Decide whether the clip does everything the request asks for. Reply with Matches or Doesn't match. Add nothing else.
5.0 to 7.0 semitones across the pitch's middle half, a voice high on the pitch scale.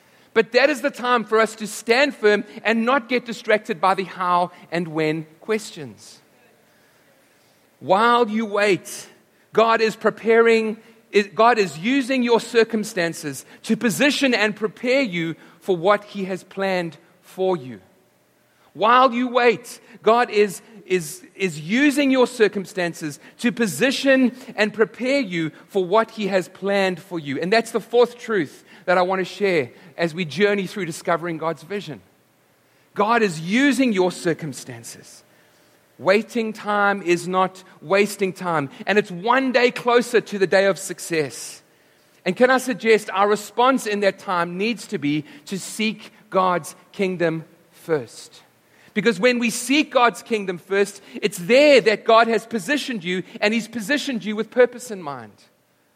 Doesn't match